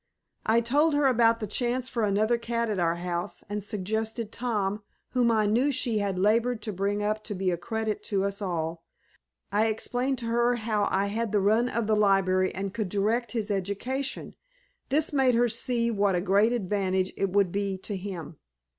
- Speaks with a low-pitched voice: No, high, 215 Hz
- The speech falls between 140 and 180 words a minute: No, average, 195 wpm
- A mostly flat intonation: No, average, 3.1 semitones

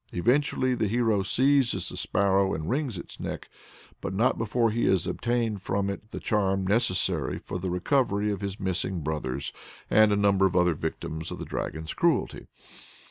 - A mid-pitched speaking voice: No, low, 100 Hz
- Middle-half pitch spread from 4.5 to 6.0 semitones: No, average, 3.9 semitones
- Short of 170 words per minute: No, average, 175 wpm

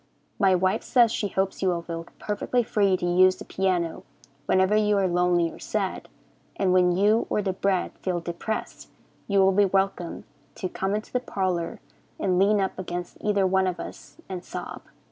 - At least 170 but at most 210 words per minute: Yes, average, 185 wpm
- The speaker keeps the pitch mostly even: Yes, narrow, 2.0 semitones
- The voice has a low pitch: No, high, 190 Hz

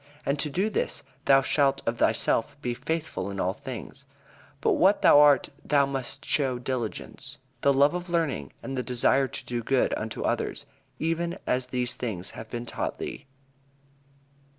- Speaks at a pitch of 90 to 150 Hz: Yes, low, 135 Hz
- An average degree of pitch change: Yes, average, 3.1 semitones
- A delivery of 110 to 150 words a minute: No, average, 170 wpm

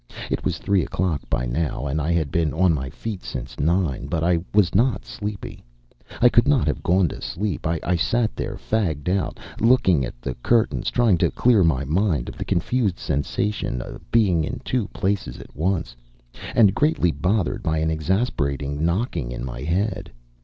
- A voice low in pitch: Yes, very low, 85 Hz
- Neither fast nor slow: Yes, average, 180 wpm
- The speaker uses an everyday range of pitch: No, wide, 5.8 semitones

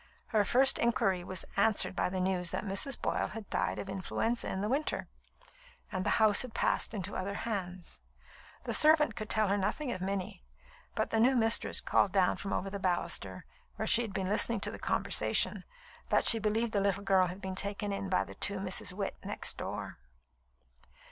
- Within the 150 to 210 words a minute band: Yes, average, 195 wpm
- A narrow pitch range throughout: No, average, 3.0 semitones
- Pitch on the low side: No, high, 200 Hz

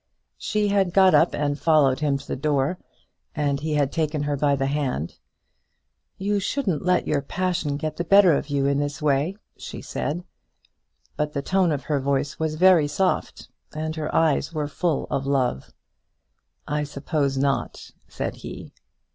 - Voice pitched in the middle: Yes, medium, 150 Hz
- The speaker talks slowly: No, average, 170 wpm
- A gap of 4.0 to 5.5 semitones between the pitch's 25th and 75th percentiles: No, average, 3.4 semitones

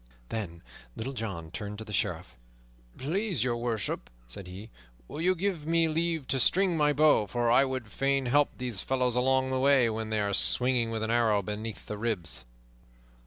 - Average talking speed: Yes, average, 185 wpm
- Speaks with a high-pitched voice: No, low, 120 Hz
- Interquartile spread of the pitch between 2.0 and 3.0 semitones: No, average, 4.4 semitones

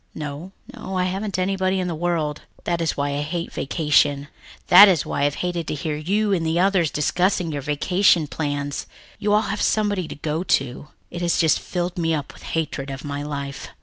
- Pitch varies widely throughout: No, average, 3.9 semitones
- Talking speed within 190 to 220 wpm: Yes, fast, 205 wpm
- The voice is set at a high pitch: No, medium, 165 Hz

